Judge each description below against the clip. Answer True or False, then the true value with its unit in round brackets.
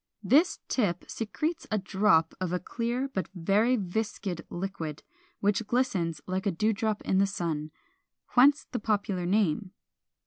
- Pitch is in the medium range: False (200 Hz)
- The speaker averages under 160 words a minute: True (145 wpm)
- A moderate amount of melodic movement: True (3.9 semitones)